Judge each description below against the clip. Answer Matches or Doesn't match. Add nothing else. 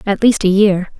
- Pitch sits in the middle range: Doesn't match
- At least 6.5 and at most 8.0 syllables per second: Doesn't match